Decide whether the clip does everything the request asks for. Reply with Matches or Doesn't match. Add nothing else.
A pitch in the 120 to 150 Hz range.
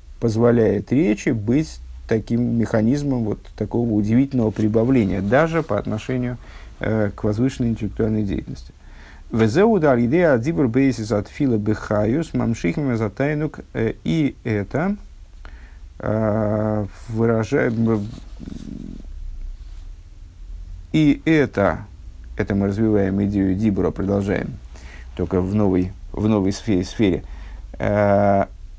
Doesn't match